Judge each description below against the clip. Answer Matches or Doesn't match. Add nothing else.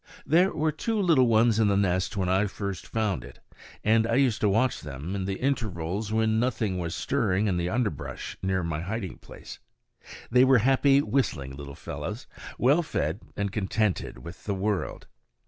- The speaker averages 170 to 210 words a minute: Matches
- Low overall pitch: Matches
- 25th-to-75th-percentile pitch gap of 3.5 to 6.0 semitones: Matches